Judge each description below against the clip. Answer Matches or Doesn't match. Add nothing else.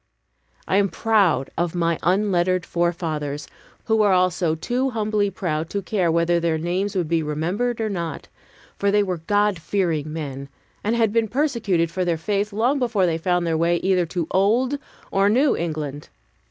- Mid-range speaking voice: Matches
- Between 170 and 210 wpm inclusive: Matches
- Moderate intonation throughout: Matches